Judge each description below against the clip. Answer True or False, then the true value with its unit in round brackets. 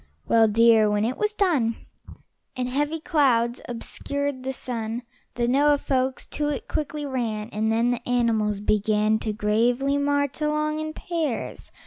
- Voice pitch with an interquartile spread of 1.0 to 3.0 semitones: False (4.3 semitones)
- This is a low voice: False (250 Hz)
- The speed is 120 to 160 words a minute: True (150 wpm)